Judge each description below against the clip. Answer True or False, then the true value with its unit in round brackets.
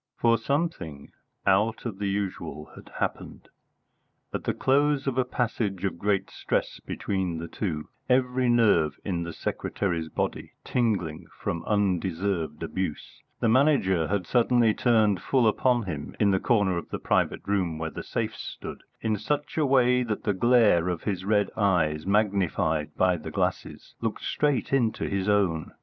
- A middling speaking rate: True (160 wpm)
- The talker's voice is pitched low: True (100 Hz)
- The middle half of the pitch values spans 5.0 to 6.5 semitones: True (5.4 semitones)